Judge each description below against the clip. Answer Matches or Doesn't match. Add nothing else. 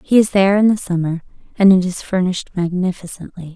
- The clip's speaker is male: Doesn't match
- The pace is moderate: Matches